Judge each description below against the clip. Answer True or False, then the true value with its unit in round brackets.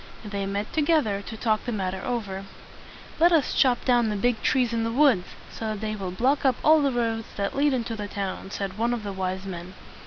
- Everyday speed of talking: False (225 wpm)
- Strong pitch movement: False (3.9 semitones)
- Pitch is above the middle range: True (220 Hz)